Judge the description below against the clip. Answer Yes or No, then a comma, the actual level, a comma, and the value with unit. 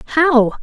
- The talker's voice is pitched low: No, very high, 275 Hz